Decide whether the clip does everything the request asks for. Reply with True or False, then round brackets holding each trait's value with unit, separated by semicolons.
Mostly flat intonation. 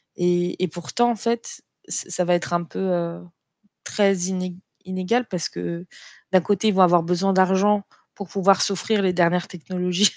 True (2.0 semitones)